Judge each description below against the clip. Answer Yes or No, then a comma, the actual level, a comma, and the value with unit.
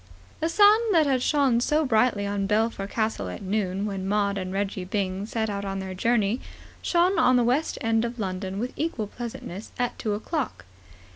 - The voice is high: Yes, high, 215 Hz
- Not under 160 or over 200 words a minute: Yes, average, 190 wpm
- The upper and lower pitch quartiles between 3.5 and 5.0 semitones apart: Yes, average, 4.2 semitones